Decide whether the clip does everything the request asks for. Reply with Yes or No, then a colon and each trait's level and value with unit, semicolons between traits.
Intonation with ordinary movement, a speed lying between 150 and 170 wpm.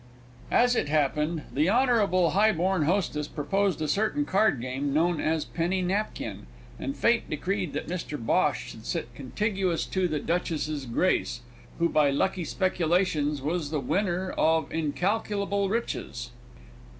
No: average, 4.6 semitones; slow, 135 wpm